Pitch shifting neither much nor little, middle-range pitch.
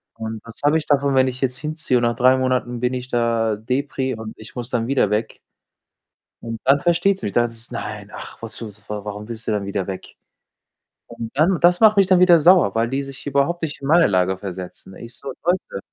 No: average, 4.4 semitones; low, 125 Hz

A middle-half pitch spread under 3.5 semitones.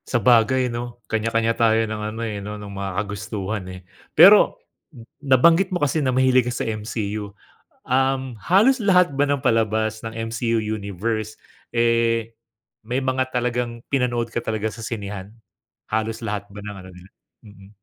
Yes: average, 2.9 semitones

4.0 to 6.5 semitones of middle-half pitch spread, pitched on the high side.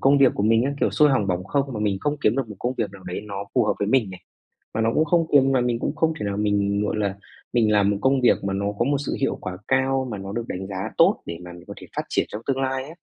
No: average, 4.9 semitones; low, 110 Hz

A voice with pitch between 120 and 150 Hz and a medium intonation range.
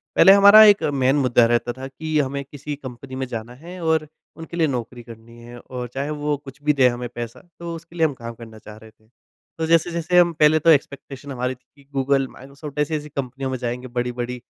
Yes: low, 135 Hz; average, 3.8 semitones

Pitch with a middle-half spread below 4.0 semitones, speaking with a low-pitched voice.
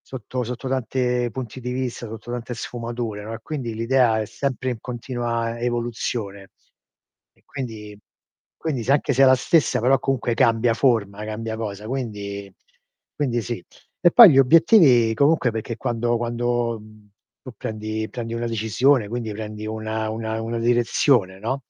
Yes: narrow, 2.5 semitones; low, 120 Hz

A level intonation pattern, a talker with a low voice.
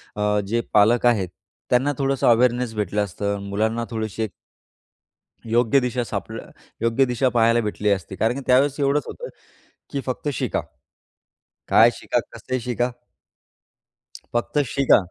No: average, 3.4 semitones; low, 120 Hz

